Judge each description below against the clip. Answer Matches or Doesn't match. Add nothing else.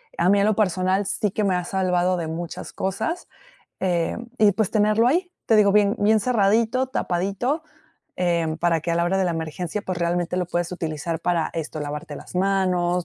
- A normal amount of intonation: Matches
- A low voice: Doesn't match